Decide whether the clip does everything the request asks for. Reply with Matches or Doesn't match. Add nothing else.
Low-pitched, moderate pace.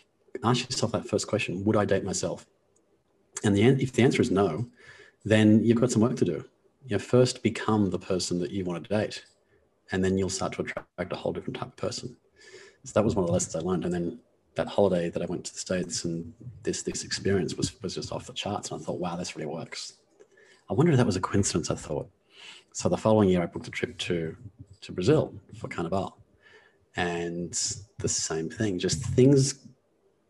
Doesn't match